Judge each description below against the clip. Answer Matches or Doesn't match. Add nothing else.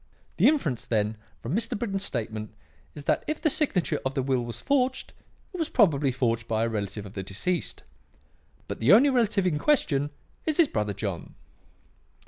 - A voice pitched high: Doesn't match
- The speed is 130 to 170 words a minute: Doesn't match